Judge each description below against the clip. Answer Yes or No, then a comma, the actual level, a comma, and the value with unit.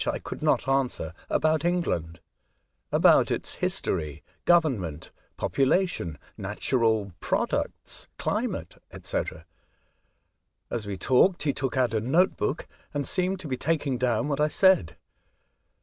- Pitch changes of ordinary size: No, wide, 6.9 semitones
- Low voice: Yes, low, 130 Hz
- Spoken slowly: Yes, slow, 125 wpm